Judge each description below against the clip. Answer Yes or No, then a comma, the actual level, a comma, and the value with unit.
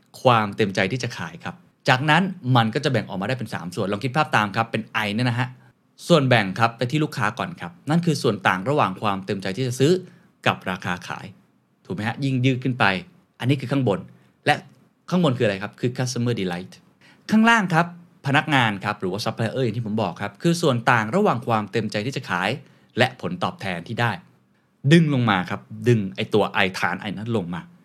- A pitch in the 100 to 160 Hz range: Yes, low, 120 Hz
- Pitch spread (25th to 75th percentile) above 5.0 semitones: Yes, wide, 5.4 semitones